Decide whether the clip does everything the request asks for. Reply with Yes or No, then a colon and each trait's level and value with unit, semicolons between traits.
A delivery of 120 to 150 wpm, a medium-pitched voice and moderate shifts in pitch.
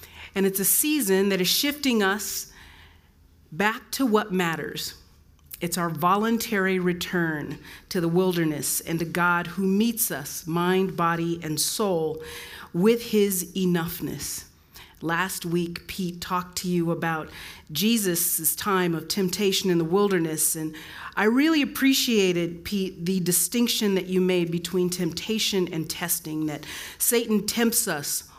Yes: slow, 135 wpm; medium, 180 Hz; average, 3.2 semitones